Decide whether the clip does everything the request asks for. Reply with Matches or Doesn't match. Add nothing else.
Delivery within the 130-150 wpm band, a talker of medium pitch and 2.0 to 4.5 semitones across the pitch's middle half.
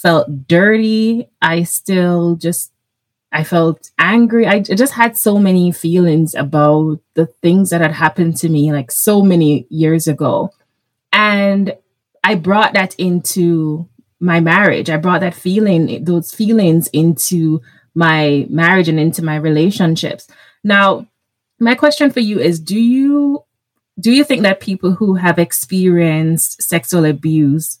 Matches